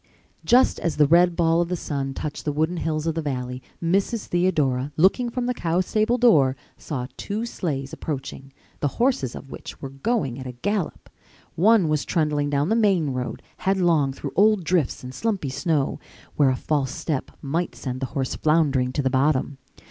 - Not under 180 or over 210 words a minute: Yes, average, 185 wpm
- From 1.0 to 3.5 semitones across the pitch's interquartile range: No, average, 5.2 semitones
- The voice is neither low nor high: Yes, medium, 155 Hz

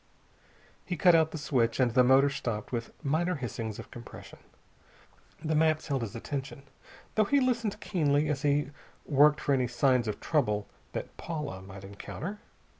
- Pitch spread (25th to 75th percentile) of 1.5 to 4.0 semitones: No, average, 4.8 semitones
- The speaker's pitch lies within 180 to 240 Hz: No, medium, 140 Hz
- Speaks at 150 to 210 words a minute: Yes, average, 165 wpm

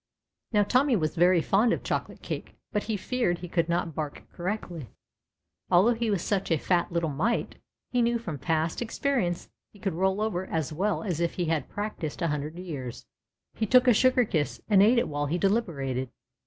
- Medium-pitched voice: Yes, medium, 180 Hz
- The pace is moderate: Yes, average, 195 wpm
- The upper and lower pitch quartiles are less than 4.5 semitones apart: No, average, 5.2 semitones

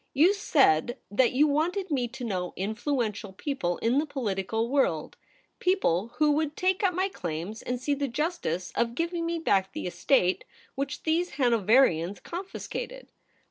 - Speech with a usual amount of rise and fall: No, wide, 7.9 semitones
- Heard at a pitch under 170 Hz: No, very high, 265 Hz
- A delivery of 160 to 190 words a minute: Yes, average, 165 wpm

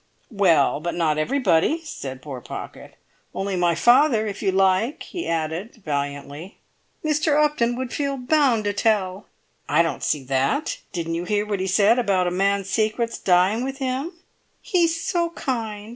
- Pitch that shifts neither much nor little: No, wide, 6.8 semitones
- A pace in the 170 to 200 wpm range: No, average, 160 wpm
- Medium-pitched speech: No, high, 205 Hz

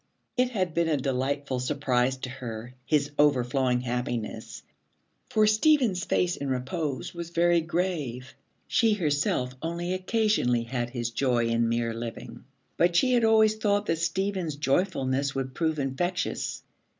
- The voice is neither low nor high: Yes, medium, 145 Hz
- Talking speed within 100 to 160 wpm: Yes, average, 140 wpm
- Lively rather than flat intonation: Yes, wide, 6.2 semitones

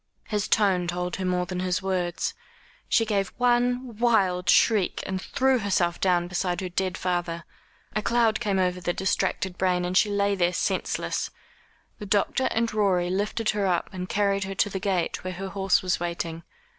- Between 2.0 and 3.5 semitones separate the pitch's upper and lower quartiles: Yes, narrow, 2.6 semitones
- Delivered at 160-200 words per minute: Yes, average, 180 wpm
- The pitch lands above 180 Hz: Yes, high, 190 Hz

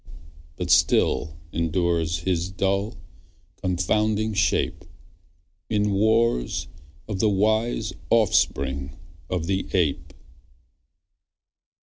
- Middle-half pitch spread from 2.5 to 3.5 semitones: No, average, 4.3 semitones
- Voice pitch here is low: Yes, very low, 95 Hz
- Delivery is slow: Yes, slow, 80 wpm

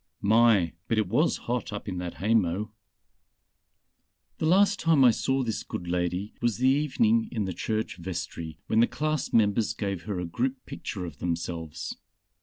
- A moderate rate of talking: Yes, average, 170 wpm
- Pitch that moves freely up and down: Yes, wide, 6.4 semitones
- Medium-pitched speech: No, low, 110 Hz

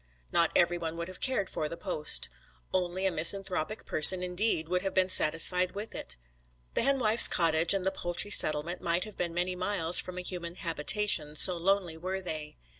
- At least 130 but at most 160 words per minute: No, average, 190 wpm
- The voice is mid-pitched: Yes, medium, 180 Hz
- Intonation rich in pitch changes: No, narrow, 2.4 semitones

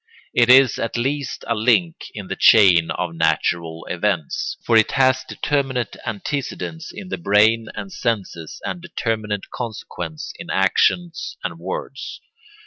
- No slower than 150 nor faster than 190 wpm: No, slow, 135 wpm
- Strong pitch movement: Yes, wide, 6.3 semitones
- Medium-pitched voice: No, low, 115 Hz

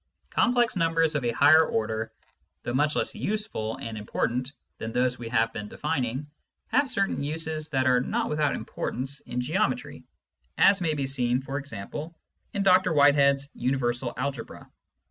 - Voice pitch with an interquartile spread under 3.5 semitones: No, average, 4.7 semitones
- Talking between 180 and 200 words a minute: No, average, 160 wpm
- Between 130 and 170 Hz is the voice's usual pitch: Yes, medium, 140 Hz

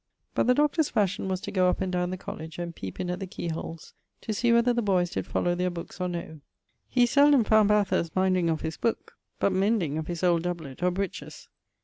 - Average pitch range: Yes, average, 3.6 semitones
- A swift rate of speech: Yes, fast, 235 wpm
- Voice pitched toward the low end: No, medium, 185 Hz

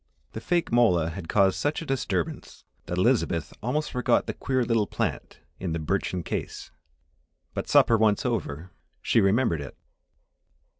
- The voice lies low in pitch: Yes, low, 105 Hz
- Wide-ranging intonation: Yes, wide, 6.1 semitones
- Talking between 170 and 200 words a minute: No, average, 150 wpm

